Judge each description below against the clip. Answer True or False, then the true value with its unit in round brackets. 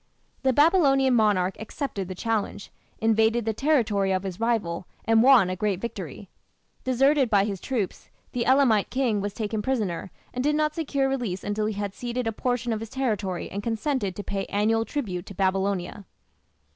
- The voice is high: True (220 Hz)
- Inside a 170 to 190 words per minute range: True (175 wpm)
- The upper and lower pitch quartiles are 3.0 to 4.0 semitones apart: False (4.5 semitones)